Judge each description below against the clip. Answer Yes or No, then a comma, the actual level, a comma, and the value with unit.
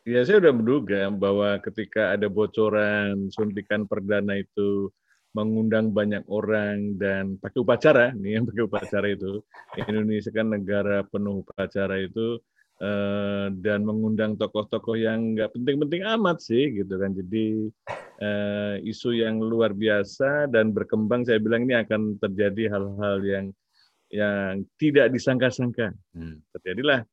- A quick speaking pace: No, average, 125 wpm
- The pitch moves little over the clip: Yes, narrow, 2.0 semitones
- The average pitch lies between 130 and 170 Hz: No, low, 105 Hz